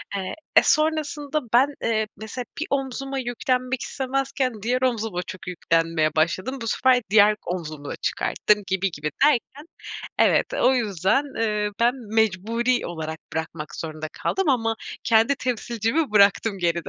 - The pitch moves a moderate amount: No, wide, 5.8 semitones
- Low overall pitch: No, high, 225 Hz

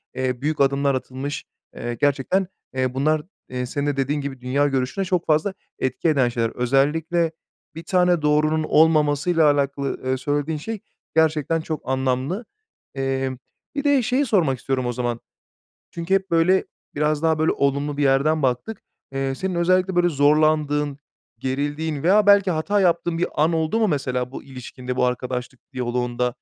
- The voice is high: No, medium, 145 Hz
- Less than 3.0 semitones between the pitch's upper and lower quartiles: No, average, 3.8 semitones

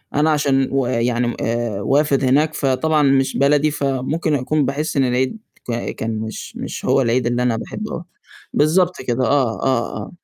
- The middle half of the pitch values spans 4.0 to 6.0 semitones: No, average, 3.6 semitones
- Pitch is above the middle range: No, low, 135 Hz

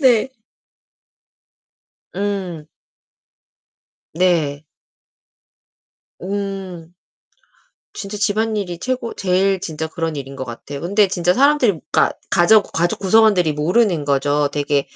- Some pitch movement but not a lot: Yes, average, 4.8 semitones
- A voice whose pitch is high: No, medium, 180 Hz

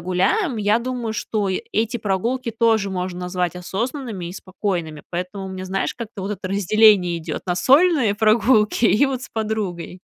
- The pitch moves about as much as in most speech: Yes, average, 3.8 semitones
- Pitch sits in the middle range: No, high, 205 Hz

